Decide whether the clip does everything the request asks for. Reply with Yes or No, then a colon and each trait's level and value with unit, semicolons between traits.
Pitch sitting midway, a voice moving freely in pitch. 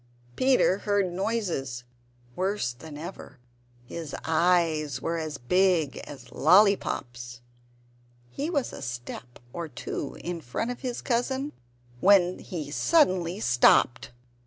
Yes: medium, 170 Hz; wide, 6.6 semitones